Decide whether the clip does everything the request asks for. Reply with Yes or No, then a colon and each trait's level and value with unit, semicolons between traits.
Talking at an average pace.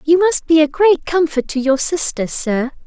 No: fast, 210 wpm